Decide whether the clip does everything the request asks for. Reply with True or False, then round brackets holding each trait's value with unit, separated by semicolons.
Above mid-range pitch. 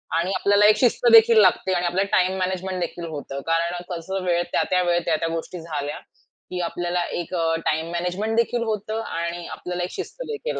False (180 Hz)